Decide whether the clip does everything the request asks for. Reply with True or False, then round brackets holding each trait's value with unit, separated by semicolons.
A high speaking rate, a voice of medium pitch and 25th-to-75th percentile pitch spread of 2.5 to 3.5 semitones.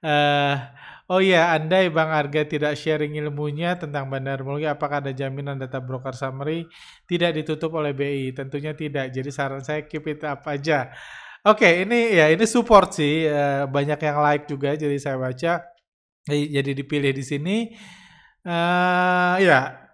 True (165 wpm; 150 Hz; 3.2 semitones)